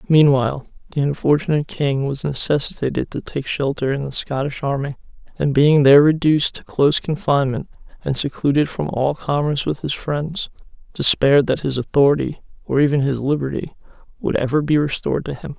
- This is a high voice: No, medium, 140 Hz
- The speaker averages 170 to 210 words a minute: No, average, 160 wpm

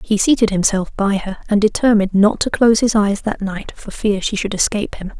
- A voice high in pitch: Yes, high, 205 Hz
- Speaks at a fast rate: Yes, fast, 230 wpm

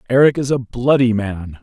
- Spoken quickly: No, average, 185 wpm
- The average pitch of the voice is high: No, low, 120 Hz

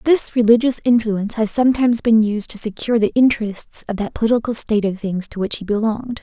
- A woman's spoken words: Yes, female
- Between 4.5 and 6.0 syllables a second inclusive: No, 6.3 syllables/s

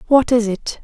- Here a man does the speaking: No, female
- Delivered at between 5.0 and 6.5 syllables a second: No, 4.6 syllables/s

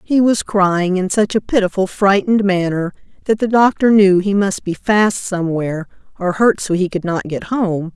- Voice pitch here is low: No, high, 195 Hz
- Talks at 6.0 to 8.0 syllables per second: No, 4.9 syllables/s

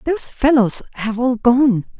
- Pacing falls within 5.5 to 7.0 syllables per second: No, 4.4 syllables/s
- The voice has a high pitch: Yes, high, 240 Hz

